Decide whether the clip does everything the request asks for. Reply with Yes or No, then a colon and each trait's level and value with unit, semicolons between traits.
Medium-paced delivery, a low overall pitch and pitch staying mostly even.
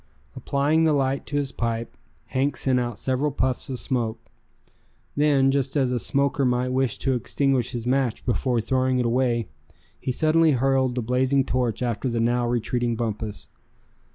Yes: average, 165 wpm; low, 130 Hz; narrow, 2.2 semitones